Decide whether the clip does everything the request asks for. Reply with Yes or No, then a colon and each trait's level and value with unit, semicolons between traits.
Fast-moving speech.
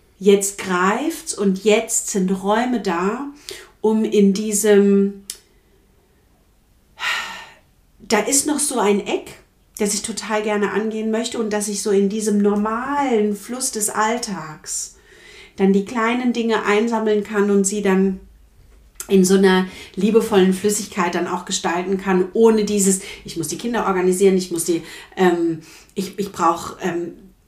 No: average, 140 wpm